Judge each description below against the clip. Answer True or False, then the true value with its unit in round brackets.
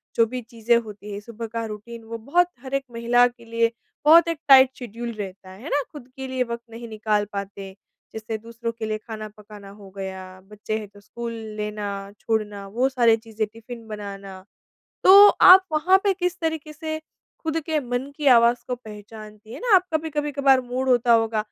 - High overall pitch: True (230 Hz)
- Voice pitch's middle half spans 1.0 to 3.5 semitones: False (4.0 semitones)